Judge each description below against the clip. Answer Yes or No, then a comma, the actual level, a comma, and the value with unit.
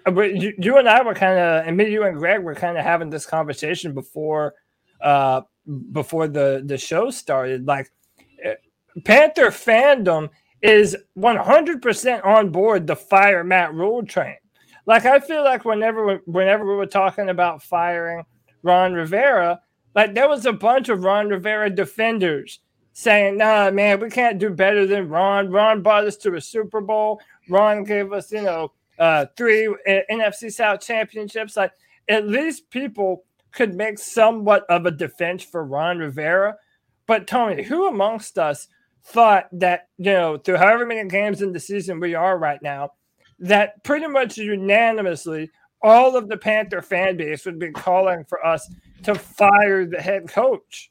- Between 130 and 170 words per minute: Yes, average, 165 wpm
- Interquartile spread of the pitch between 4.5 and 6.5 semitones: No, average, 3.9 semitones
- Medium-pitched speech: No, high, 200 Hz